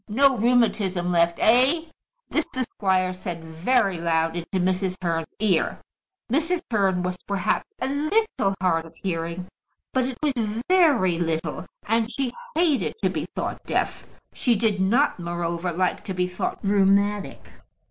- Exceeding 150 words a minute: No, average, 145 wpm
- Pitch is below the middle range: No, high, 195 Hz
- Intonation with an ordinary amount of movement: No, wide, 5.8 semitones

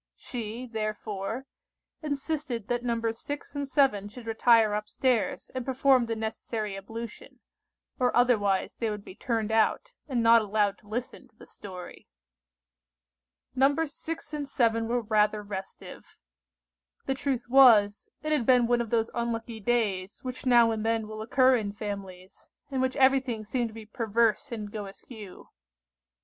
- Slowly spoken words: No, average, 155 wpm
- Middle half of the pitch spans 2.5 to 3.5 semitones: Yes, average, 3.2 semitones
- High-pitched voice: Yes, high, 230 Hz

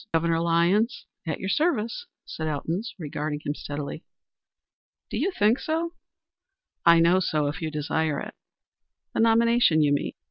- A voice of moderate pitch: Yes, medium, 170 Hz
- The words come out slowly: No, average, 145 wpm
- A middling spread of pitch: No, wide, 6.6 semitones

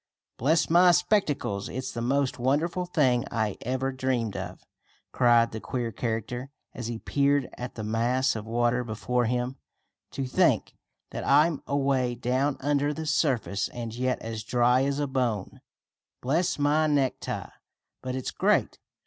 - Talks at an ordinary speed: Yes, average, 150 wpm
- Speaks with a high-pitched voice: No, low, 130 Hz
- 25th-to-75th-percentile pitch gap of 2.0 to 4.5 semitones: Yes, average, 3.1 semitones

